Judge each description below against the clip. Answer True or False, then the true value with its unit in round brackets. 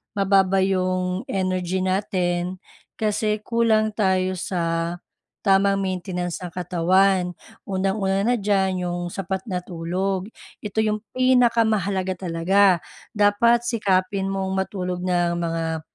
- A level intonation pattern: True (1.9 semitones)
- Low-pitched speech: False (190 Hz)